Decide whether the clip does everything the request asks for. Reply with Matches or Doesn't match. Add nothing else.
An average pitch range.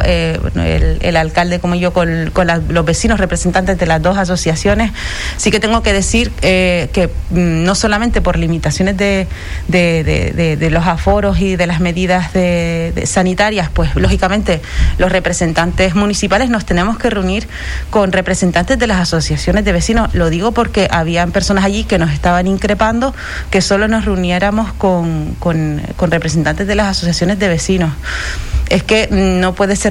Matches